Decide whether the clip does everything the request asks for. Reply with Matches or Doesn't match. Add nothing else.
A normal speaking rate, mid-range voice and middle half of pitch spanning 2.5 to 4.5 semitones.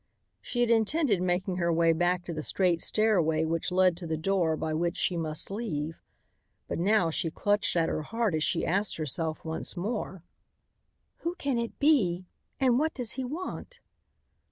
Doesn't match